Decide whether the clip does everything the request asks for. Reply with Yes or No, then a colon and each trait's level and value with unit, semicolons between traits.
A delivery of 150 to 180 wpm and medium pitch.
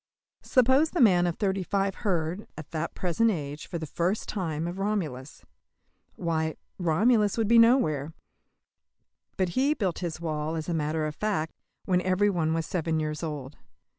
Yes: average, 165 wpm; medium, 175 Hz